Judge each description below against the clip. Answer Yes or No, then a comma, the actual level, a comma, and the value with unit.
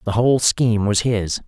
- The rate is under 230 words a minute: Yes, fast, 205 wpm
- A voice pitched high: No, low, 110 Hz